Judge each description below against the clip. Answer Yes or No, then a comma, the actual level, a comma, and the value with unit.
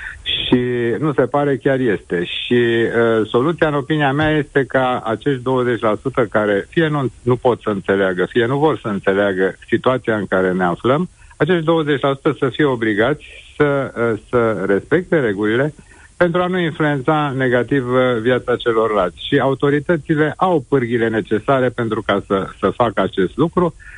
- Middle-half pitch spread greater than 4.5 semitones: Yes, average, 4.9 semitones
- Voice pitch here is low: Yes, low, 125 Hz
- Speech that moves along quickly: No, average, 155 wpm